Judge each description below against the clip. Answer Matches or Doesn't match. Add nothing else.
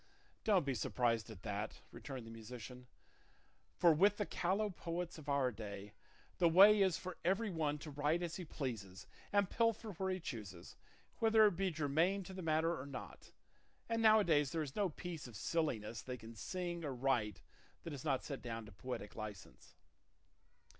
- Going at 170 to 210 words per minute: Matches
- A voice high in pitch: Doesn't match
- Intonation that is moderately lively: Doesn't match